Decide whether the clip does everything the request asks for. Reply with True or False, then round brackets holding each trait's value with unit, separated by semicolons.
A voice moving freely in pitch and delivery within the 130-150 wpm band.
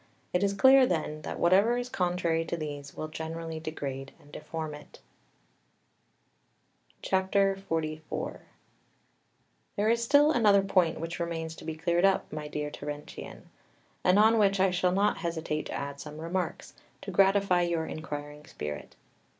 False (4.1 semitones; 145 wpm)